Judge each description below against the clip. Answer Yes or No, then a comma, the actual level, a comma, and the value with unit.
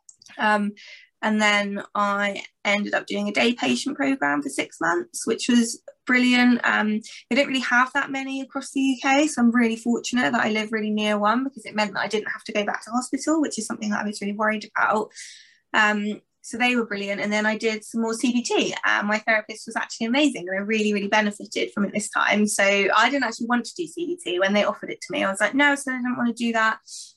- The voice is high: Yes, high, 225 Hz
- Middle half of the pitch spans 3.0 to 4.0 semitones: Yes, average, 3.4 semitones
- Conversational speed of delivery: No, fast, 245 wpm